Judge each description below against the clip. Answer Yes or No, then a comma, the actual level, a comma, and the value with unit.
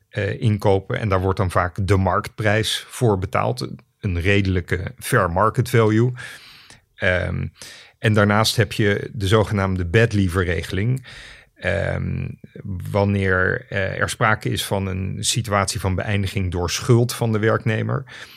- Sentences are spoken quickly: No, slow, 135 wpm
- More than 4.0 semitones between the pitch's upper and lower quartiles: No, average, 3.3 semitones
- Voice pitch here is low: Yes, low, 105 Hz